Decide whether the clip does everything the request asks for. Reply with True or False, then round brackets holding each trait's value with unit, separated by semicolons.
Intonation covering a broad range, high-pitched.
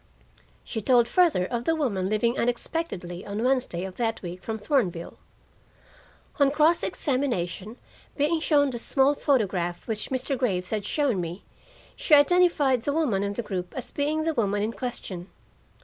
True (6.5 semitones; 240 Hz)